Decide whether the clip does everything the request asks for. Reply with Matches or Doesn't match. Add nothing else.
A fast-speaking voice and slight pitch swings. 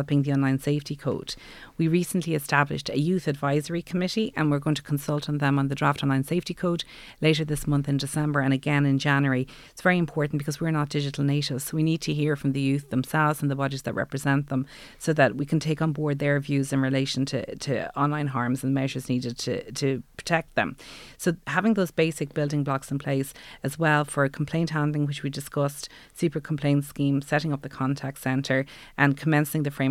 Matches